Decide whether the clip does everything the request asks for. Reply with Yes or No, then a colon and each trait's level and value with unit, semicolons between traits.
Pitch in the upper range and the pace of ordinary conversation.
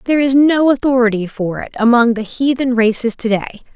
Yes: high, 240 Hz; average, 190 wpm